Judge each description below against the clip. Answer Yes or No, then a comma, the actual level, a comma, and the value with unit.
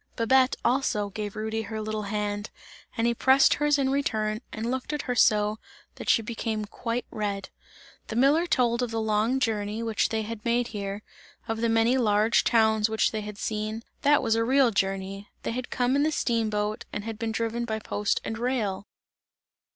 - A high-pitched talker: Yes, high, 225 Hz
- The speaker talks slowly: No, average, 195 wpm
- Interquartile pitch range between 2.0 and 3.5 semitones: Yes, narrow, 2.4 semitones